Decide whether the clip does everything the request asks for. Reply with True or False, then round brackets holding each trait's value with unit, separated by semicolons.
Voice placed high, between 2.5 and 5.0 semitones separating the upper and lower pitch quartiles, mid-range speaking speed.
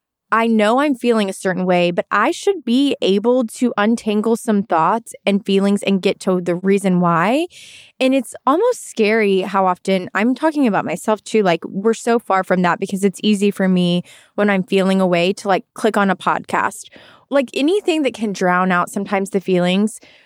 True (205 Hz; 3.7 semitones; 195 wpm)